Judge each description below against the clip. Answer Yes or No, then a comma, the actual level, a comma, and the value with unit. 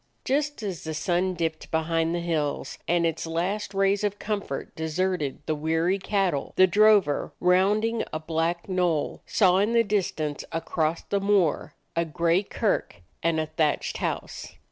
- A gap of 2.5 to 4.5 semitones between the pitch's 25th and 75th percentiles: Yes, average, 3.6 semitones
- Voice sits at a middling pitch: Yes, medium, 175 Hz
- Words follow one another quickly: No, average, 155 wpm